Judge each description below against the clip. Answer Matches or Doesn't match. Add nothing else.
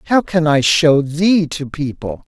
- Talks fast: Doesn't match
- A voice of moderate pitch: Matches